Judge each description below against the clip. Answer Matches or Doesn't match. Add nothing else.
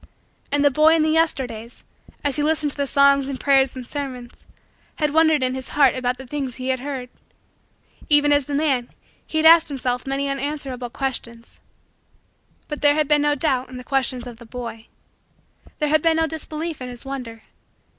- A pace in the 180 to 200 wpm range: Matches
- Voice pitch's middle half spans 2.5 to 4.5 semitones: Matches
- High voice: Matches